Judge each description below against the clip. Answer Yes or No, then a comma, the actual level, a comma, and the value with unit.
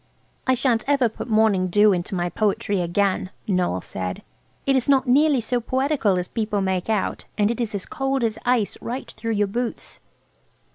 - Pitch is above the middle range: Yes, high, 220 Hz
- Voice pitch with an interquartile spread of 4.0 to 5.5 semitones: Yes, average, 4.5 semitones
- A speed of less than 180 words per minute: No, average, 185 wpm